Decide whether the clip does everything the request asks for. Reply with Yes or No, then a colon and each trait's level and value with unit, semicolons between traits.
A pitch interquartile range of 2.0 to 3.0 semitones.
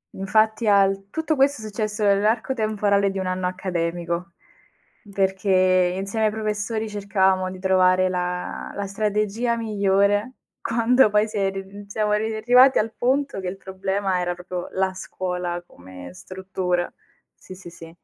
Yes: narrow, 2.5 semitones